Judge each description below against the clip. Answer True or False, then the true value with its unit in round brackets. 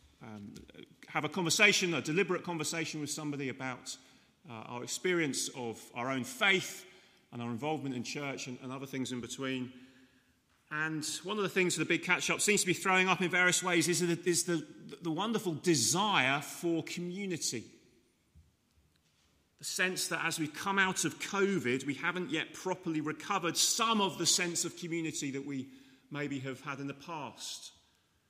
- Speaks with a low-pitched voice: False (155 Hz)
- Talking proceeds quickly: False (175 wpm)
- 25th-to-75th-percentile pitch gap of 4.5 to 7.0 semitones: True (5.2 semitones)